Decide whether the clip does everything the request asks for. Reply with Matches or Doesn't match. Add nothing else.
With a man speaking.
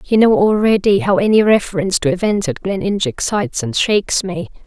Doesn't match